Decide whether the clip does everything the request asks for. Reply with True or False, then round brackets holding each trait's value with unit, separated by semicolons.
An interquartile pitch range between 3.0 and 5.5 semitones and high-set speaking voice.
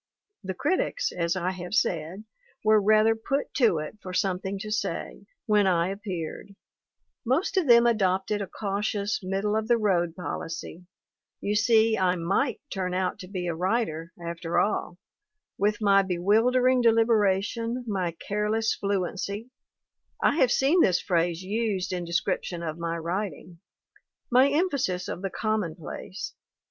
True (3.8 semitones; 200 Hz)